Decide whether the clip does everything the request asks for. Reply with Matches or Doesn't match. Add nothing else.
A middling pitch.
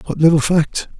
Matches